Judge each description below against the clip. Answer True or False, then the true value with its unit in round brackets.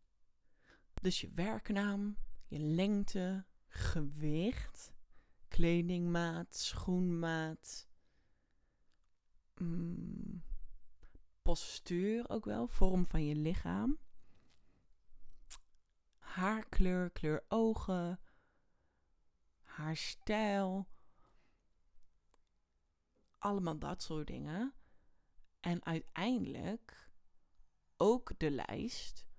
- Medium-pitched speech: True (170 Hz)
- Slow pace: True (55 wpm)